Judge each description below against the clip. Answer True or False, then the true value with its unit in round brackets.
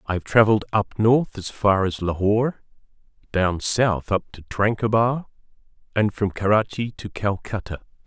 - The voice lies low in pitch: True (105 Hz)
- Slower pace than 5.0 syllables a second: True (4.6 syllables/s)